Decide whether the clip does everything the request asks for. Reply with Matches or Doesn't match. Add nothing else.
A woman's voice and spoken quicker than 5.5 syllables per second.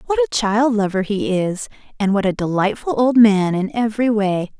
Doesn't match